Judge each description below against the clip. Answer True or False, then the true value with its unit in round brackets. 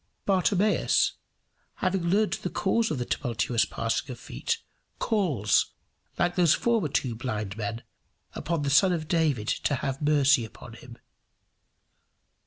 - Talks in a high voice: False (145 Hz)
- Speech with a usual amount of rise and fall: False (7.3 semitones)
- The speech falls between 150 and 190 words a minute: False (135 wpm)